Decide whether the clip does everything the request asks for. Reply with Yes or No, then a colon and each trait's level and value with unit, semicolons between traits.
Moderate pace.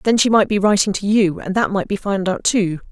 No: fast, 290 wpm